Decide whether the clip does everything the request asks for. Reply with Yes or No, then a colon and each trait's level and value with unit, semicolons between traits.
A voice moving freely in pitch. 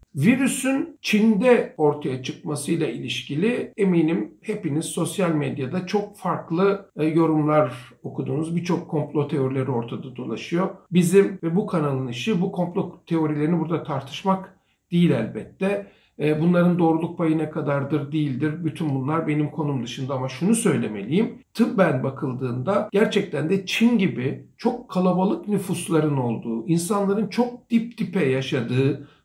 No: average, 5.0 semitones